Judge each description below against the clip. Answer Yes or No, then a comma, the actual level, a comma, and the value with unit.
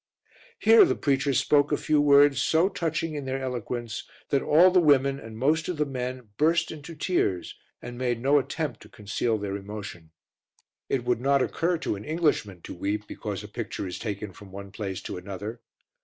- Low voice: Yes, low, 130 Hz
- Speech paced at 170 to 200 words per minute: Yes, average, 190 wpm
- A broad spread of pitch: Yes, wide, 6.0 semitones